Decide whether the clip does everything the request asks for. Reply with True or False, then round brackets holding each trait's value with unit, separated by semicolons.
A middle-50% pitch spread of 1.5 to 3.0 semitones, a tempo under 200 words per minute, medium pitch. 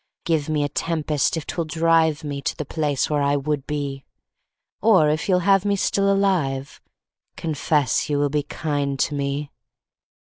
True (2.5 semitones; 170 wpm; 150 Hz)